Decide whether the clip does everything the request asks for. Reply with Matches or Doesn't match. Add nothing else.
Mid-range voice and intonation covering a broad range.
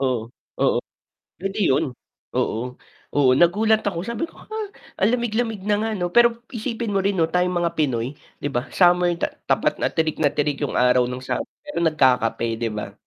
Matches